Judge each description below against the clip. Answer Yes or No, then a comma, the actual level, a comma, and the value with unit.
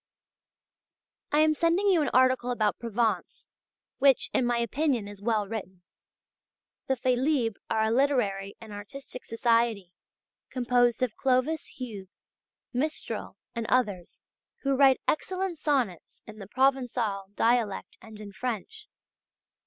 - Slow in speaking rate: Yes, slow, 125 wpm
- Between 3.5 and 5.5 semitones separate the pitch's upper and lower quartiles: Yes, average, 4.2 semitones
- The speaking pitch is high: Yes, high, 240 Hz